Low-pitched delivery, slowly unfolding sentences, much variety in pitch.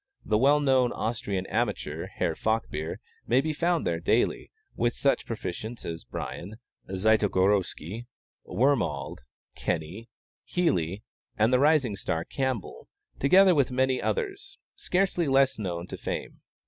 Yes: low, 120 Hz; slow, 125 wpm; wide, 6.6 semitones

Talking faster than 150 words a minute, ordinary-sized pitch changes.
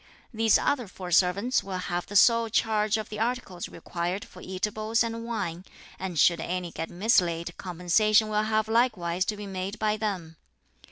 Yes: average, 170 wpm; average, 3.5 semitones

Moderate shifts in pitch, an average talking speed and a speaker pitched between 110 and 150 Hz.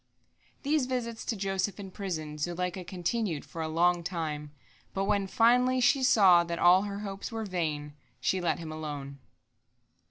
No: average, 4.3 semitones; average, 160 wpm; medium, 185 Hz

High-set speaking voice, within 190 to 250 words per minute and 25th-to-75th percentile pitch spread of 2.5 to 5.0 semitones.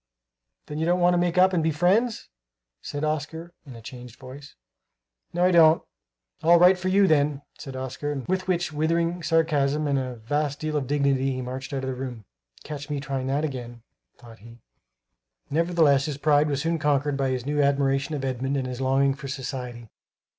No: medium, 145 Hz; average, 195 wpm; average, 3.4 semitones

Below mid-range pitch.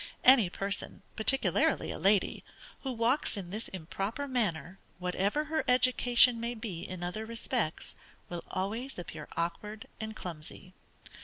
No: high, 215 Hz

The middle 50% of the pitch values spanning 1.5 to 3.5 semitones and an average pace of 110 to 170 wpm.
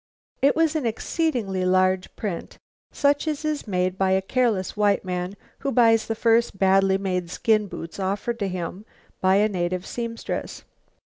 No: average, 4.1 semitones; average, 160 wpm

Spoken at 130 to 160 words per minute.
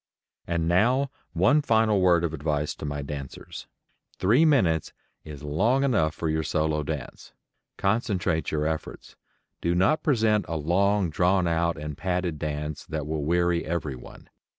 Yes: average, 150 wpm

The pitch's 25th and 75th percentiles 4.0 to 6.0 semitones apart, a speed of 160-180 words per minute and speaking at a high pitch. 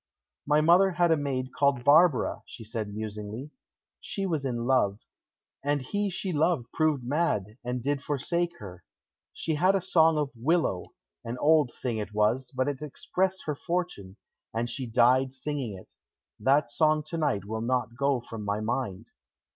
No: average, 5.1 semitones; average, 170 wpm; low, 135 Hz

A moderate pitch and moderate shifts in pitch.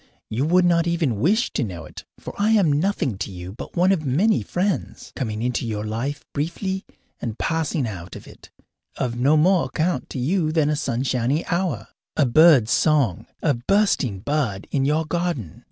No: medium, 145 Hz; wide, 6.5 semitones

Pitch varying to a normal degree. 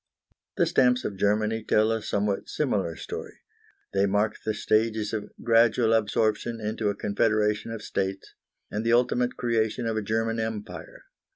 No: narrow, 1.5 semitones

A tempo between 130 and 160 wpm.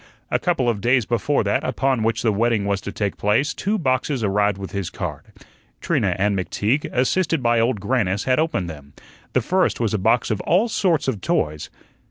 No: average, 200 wpm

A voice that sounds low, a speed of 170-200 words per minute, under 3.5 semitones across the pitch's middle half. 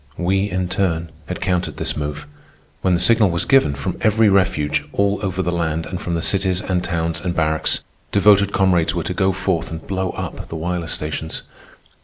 Yes: very low, 90 Hz; average, 195 wpm; average, 2.7 semitones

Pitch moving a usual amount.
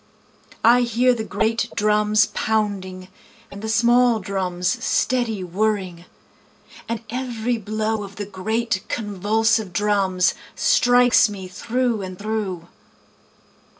Yes: average, 3.2 semitones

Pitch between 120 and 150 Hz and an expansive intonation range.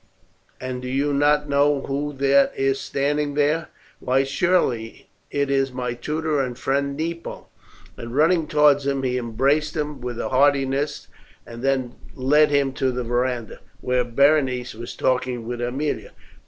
No: low, 135 Hz; narrow, 2.6 semitones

